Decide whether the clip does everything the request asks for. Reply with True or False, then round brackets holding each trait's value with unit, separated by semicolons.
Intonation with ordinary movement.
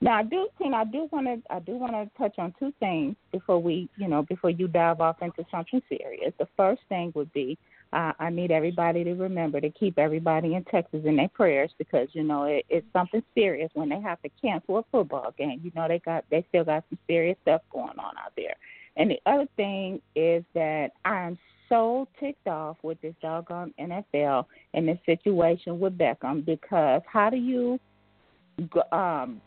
True (4.6 semitones)